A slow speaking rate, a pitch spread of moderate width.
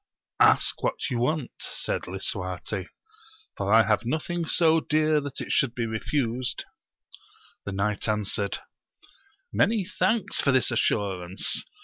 No: slow, 125 wpm; wide, 7.1 semitones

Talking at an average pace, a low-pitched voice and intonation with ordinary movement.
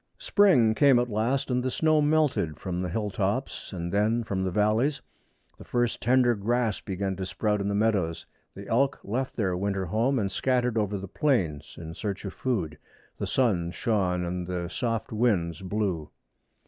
Yes: average, 180 wpm; low, 105 Hz; average, 4.8 semitones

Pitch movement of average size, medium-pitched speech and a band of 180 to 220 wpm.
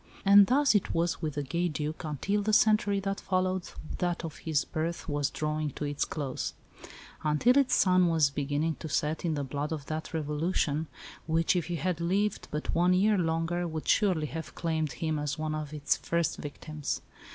Yes: average, 3.2 semitones; medium, 160 Hz; average, 190 wpm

